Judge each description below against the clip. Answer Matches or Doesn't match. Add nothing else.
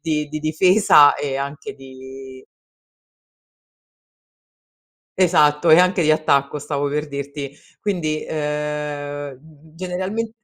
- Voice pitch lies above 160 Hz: Doesn't match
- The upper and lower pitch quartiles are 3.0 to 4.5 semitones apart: Doesn't match